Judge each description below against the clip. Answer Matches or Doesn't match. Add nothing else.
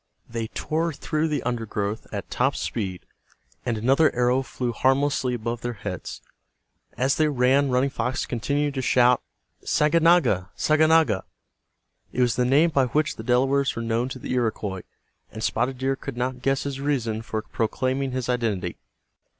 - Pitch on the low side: Matches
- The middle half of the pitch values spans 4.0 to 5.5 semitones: Doesn't match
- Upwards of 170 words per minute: Doesn't match